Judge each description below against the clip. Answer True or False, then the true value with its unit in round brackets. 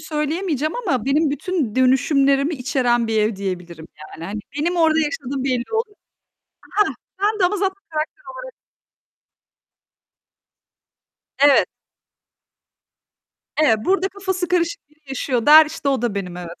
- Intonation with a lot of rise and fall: True (6.4 semitones)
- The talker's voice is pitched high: True (290 Hz)